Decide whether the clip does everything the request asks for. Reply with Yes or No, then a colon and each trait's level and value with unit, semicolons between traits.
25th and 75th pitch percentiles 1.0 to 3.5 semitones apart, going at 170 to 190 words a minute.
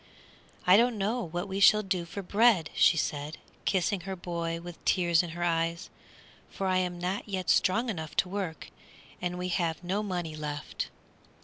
Yes: average, 2.7 semitones; average, 180 wpm